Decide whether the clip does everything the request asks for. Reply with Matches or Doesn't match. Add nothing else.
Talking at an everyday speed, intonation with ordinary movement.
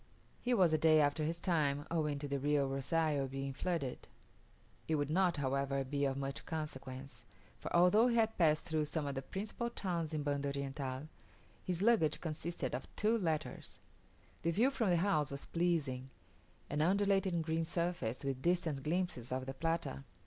Matches